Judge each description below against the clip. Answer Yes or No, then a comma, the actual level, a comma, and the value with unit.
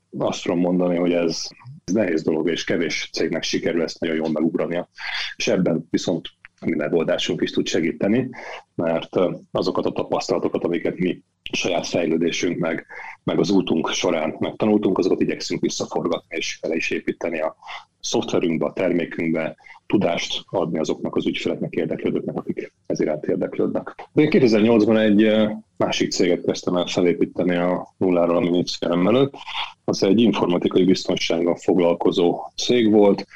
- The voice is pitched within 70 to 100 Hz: Yes, very low, 90 Hz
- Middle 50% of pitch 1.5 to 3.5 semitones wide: No, average, 3.9 semitones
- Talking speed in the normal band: Yes, average, 140 wpm